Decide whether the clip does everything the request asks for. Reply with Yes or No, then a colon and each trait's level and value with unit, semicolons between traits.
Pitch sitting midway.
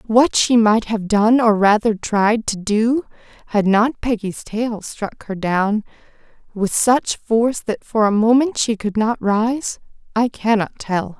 No: high, 220 Hz